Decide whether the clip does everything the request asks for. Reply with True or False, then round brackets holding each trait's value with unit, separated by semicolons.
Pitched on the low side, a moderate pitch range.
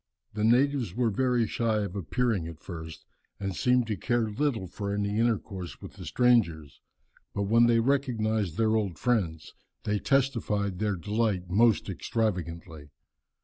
True (105 Hz; 4.1 semitones)